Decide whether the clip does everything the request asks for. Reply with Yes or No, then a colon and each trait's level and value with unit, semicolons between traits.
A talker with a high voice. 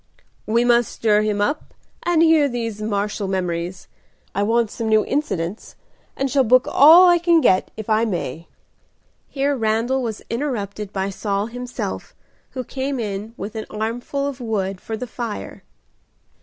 Yes: high, 225 Hz